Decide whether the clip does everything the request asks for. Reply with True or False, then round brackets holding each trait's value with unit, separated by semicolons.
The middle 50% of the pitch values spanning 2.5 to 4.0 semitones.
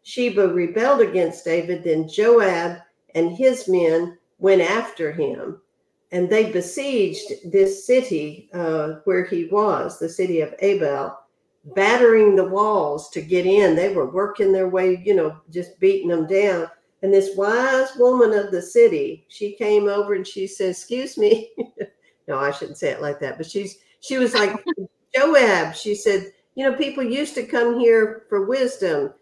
False (5.6 semitones)